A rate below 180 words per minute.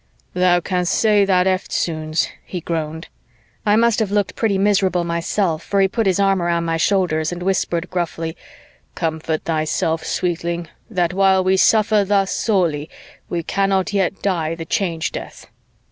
Yes: average, 155 wpm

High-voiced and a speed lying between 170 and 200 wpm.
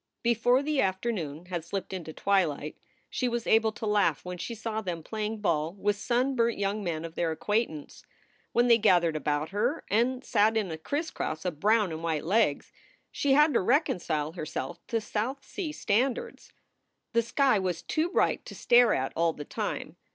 Yes: high, 205 Hz; average, 180 wpm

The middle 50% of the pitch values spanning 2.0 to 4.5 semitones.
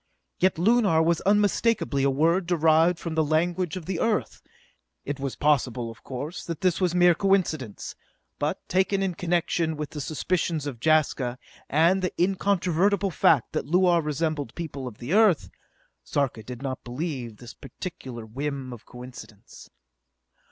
No: average, 4.9 semitones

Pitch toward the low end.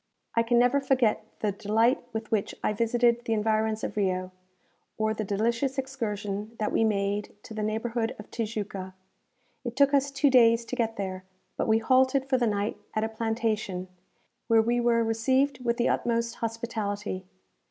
No: high, 225 Hz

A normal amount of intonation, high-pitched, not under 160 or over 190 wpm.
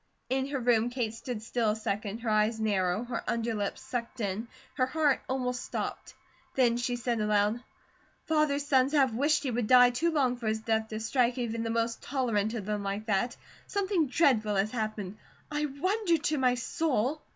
Yes: average, 3.5 semitones; high, 240 Hz; average, 185 wpm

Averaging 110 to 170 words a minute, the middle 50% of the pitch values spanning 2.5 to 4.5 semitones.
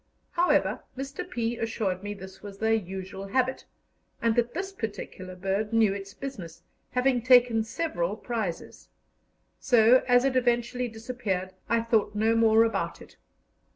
Yes: average, 145 wpm; average, 3.9 semitones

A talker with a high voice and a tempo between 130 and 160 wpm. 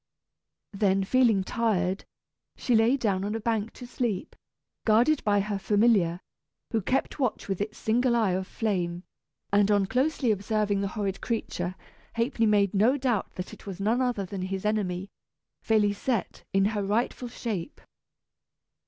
Yes: high, 210 Hz; average, 155 wpm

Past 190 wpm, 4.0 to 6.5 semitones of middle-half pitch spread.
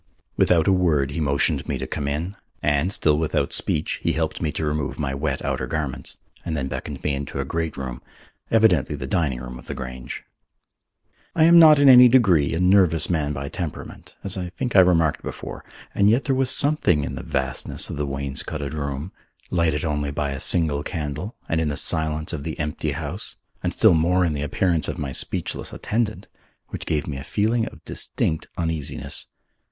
Yes: average, 200 wpm; average, 4.3 semitones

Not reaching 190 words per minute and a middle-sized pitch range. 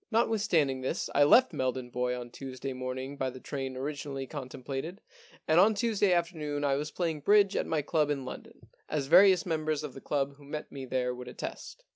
No: average, 200 wpm; average, 3.8 semitones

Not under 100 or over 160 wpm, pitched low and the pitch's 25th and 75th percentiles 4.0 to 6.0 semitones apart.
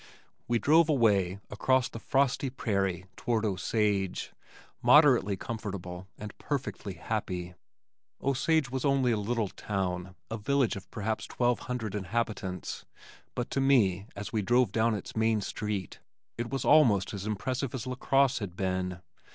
Yes: average, 145 wpm; low, 110 Hz; average, 4.6 semitones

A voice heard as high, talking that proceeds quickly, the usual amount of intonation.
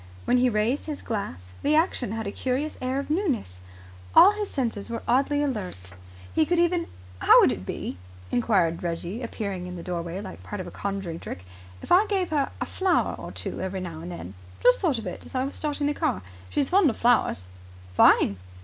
No: high, 235 Hz; fast, 210 wpm; wide, 8.4 semitones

